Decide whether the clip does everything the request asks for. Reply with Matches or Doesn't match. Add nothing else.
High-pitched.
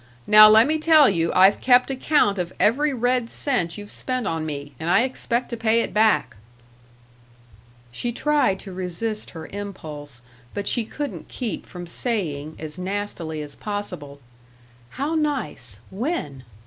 Matches